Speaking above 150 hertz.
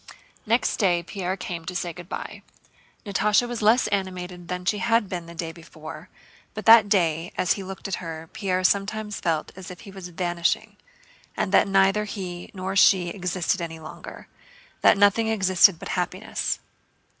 Yes: medium, 185 Hz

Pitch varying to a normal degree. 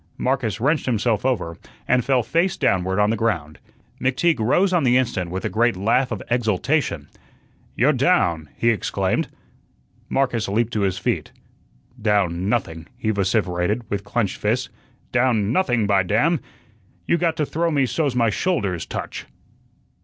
Yes: average, 5.0 semitones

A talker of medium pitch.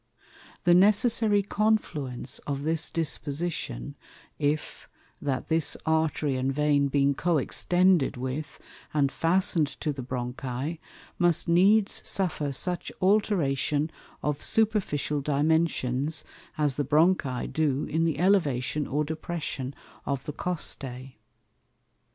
Yes: medium, 150 Hz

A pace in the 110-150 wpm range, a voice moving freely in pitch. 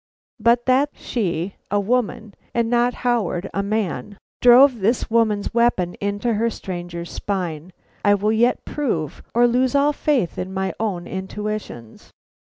No: average, 145 wpm; average, 4.1 semitones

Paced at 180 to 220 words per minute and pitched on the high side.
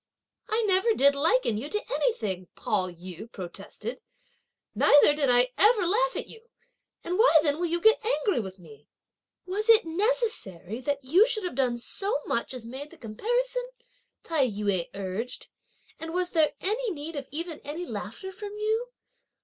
No: average, 165 wpm; very high, 315 Hz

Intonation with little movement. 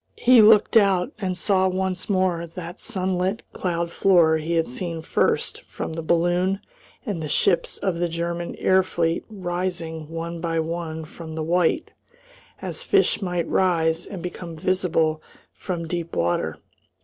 Yes: narrow, 2.2 semitones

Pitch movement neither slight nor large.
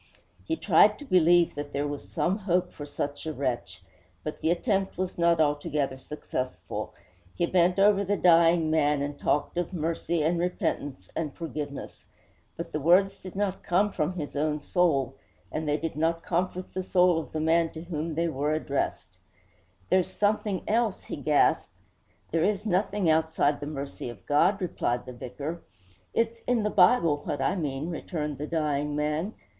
Yes: average, 3.7 semitones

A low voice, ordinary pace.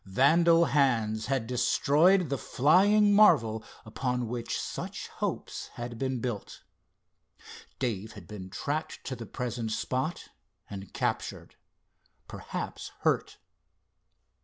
No: low, 125 Hz; slow, 110 wpm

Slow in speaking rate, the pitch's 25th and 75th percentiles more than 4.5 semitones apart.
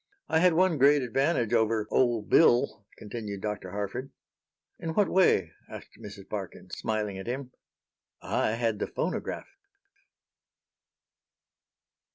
Yes: slow, 120 wpm; average, 5.3 semitones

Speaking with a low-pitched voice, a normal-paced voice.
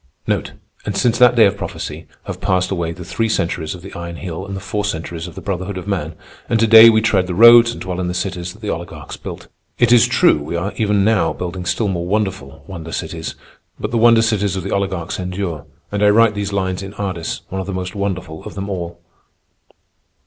No: very low, 95 Hz; fast, 230 wpm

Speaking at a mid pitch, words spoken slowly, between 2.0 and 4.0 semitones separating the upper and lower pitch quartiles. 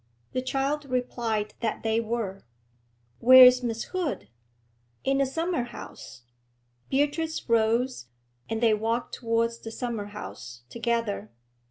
No: high, 235 Hz; slow, 125 wpm; average, 2.7 semitones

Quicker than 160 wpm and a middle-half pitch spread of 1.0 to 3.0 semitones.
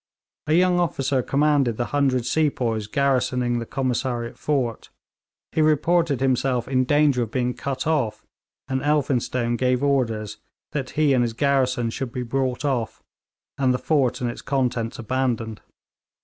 No: average, 150 wpm; narrow, 2.6 semitones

